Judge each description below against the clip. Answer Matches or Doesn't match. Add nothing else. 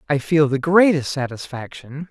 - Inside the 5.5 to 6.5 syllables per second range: Doesn't match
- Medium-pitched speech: Matches